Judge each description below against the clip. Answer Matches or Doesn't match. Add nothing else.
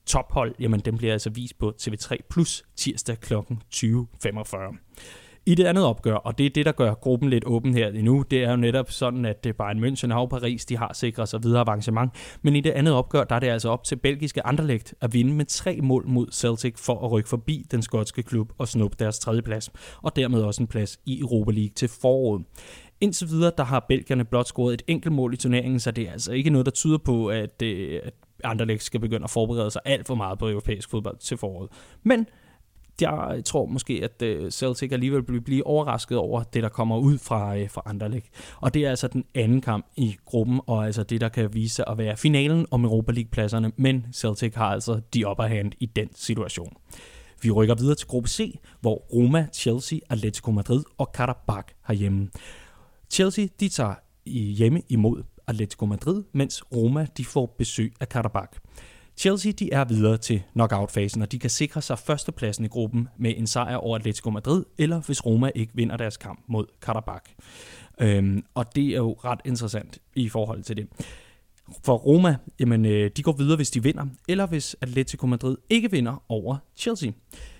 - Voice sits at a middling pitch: Doesn't match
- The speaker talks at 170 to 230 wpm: Matches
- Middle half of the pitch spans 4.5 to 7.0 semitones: Doesn't match